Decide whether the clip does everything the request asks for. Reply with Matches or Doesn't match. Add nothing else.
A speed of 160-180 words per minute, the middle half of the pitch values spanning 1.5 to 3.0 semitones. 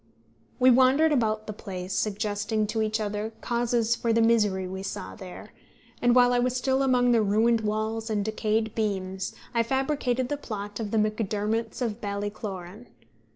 Matches